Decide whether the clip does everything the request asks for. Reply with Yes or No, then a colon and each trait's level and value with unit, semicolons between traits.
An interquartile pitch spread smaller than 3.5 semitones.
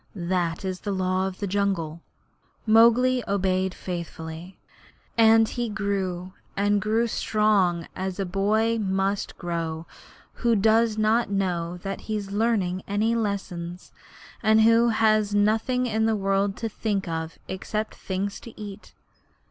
Yes: average, 2.9 semitones